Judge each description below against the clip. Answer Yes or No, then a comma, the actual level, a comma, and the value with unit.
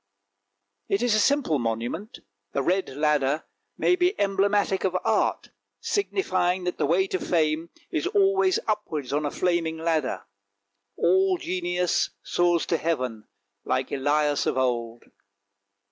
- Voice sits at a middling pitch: Yes, medium, 175 Hz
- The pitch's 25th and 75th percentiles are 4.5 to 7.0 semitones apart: Yes, average, 5.0 semitones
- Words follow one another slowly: Yes, slow, 130 wpm